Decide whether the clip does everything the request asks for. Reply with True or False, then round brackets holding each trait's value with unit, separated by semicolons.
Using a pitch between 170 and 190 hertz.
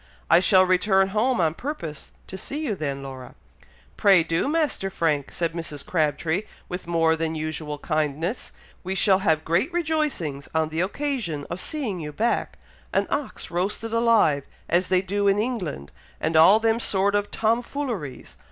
True (185 Hz)